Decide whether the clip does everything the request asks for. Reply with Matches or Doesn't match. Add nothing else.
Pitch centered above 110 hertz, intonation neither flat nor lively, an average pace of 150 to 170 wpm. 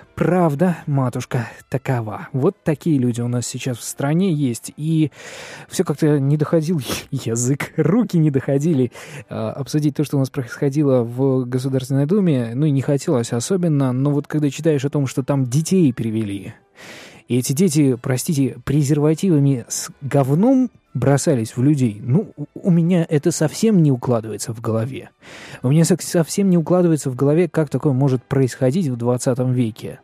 Matches